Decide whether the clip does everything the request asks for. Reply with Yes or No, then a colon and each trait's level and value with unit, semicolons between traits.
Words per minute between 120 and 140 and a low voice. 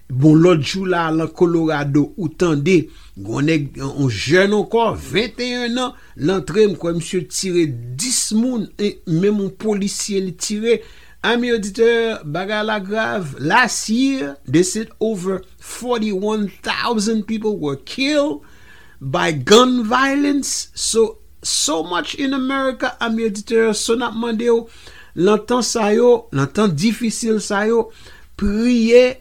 No: slow, 135 wpm; high, 215 Hz